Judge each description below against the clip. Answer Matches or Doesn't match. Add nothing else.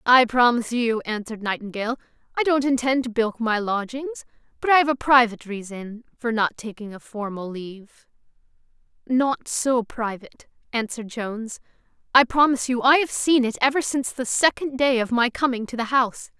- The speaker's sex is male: Doesn't match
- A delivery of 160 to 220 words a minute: Matches